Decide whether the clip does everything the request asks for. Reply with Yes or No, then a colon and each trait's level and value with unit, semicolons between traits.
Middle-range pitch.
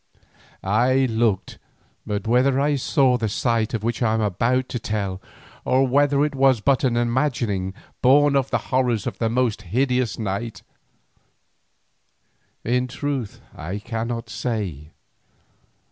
No: low, 120 Hz